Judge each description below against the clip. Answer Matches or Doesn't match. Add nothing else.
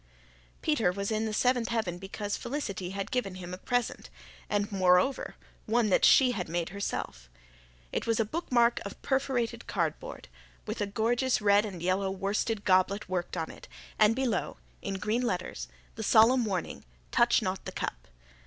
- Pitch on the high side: Matches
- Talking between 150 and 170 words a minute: Matches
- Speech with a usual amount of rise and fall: Matches